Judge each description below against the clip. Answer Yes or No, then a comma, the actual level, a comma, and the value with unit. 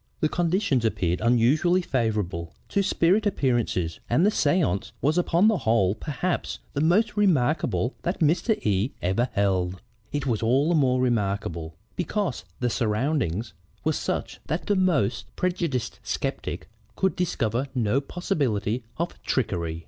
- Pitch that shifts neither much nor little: No, wide, 8.5 semitones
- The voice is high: No, low, 130 Hz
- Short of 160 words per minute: Yes, average, 140 wpm